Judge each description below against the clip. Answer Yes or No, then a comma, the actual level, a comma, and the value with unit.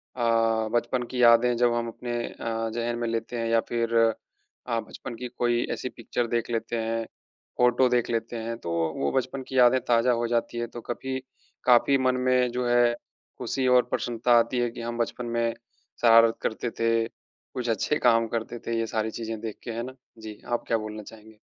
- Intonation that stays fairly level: Yes, narrow, 1.1 semitones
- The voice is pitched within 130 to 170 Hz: No, low, 120 Hz